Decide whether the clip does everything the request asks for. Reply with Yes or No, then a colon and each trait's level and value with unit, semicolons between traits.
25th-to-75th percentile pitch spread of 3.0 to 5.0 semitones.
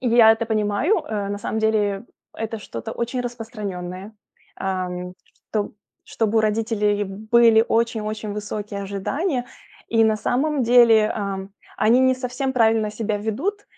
No: narrow, 2.5 semitones